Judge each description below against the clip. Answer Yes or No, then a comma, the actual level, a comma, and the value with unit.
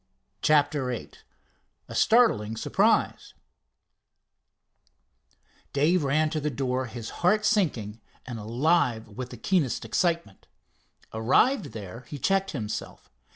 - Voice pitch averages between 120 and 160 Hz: Yes, low, 135 Hz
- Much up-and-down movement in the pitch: Yes, wide, 6.8 semitones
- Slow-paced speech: Yes, slow, 110 wpm